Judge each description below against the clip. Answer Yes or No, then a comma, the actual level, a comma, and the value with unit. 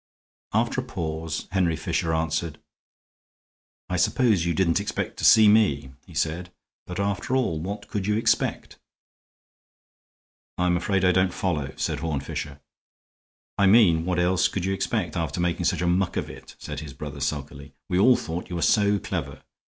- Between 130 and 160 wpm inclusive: No, average, 170 wpm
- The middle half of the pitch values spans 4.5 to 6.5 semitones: No, average, 3.3 semitones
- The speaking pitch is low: Yes, very low, 90 Hz